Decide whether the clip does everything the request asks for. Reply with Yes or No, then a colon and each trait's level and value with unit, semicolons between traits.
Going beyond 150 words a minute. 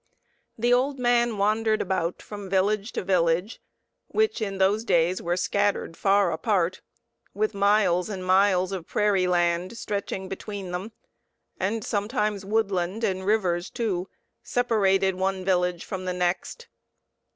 No: slow, 135 wpm